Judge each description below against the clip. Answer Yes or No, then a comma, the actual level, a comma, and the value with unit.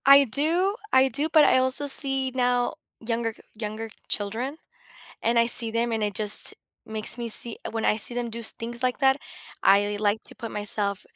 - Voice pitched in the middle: No, high, 235 Hz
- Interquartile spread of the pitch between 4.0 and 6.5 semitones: No, average, 3.2 semitones